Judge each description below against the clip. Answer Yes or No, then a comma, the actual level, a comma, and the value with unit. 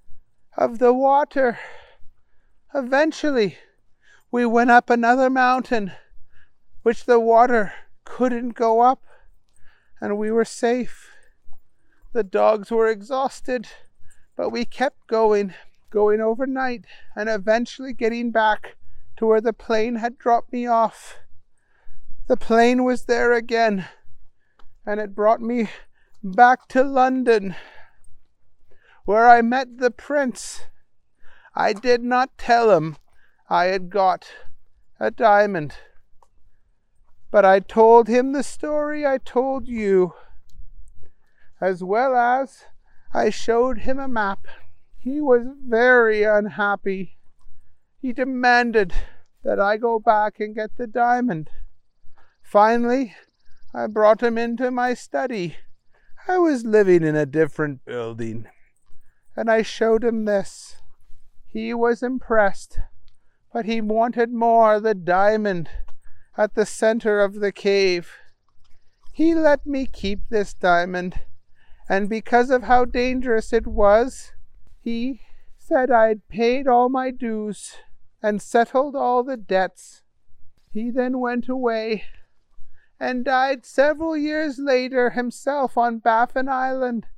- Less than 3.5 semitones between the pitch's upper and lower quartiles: No, average, 4.3 semitones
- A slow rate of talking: Yes, slow, 120 wpm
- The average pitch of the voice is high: Yes, high, 225 Hz